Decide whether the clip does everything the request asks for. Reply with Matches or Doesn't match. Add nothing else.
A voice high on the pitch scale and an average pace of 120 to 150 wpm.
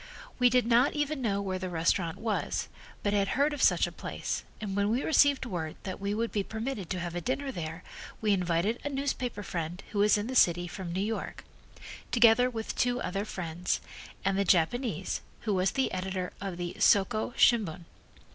Doesn't match